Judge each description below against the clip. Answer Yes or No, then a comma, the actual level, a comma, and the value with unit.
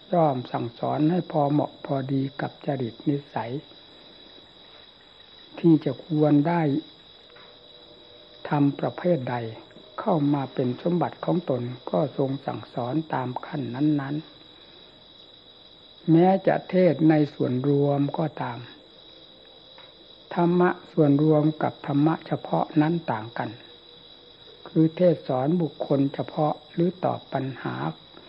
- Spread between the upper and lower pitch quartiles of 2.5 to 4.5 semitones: Yes, average, 3.6 semitones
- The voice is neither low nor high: Yes, medium, 145 Hz